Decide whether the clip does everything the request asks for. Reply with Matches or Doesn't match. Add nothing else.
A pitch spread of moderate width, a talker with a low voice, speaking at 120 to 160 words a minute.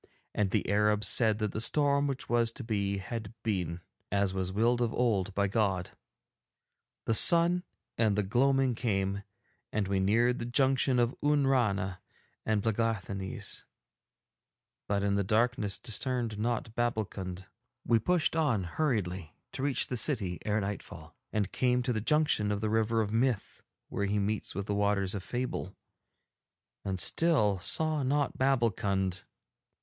Matches